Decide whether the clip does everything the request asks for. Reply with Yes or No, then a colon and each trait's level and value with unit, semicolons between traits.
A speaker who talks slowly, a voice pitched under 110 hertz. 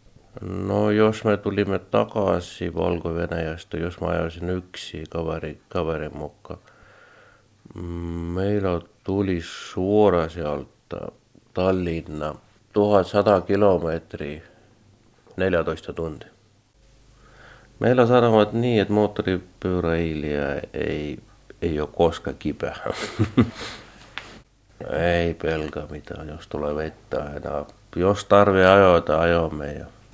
Yes: slow, 85 wpm; very low, 90 Hz